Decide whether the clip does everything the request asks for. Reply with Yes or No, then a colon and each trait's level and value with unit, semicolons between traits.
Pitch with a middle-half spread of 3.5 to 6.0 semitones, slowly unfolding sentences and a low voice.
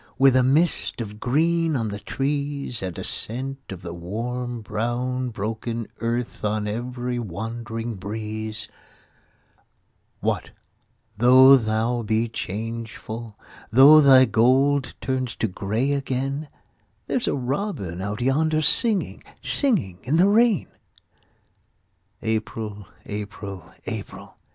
Yes: average, 3.8 semitones; slow, 110 wpm; low, 120 Hz